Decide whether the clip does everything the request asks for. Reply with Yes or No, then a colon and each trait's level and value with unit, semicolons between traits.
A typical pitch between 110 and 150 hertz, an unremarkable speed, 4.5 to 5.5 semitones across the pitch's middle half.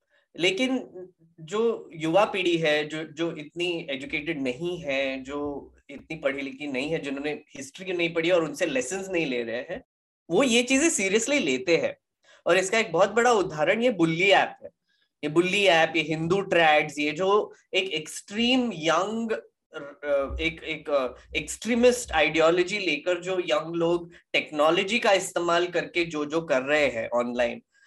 No: medium, 170 Hz; average, 155 wpm; average, 4.8 semitones